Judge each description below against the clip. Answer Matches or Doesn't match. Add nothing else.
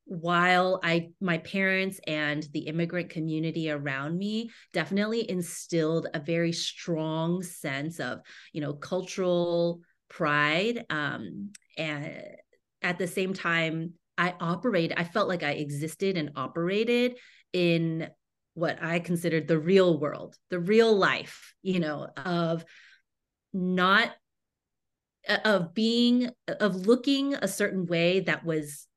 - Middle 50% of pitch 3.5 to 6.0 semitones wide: Doesn't match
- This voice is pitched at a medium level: Matches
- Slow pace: Matches